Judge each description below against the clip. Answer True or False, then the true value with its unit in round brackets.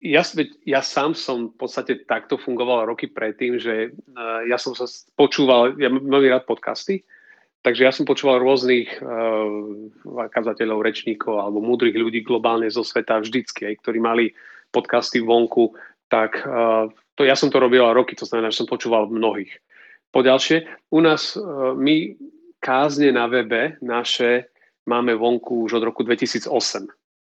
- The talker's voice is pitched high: False (120 Hz)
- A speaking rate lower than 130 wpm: False (145 wpm)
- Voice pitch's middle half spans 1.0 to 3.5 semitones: True (2.9 semitones)